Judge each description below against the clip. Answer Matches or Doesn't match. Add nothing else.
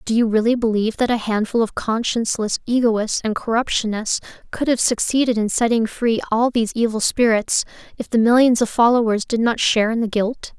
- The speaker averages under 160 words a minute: Doesn't match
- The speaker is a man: Doesn't match